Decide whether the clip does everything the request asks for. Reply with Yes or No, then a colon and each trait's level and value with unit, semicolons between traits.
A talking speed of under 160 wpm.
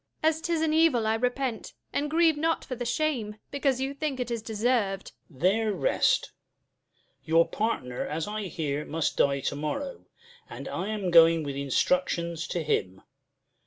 No: average, 170 wpm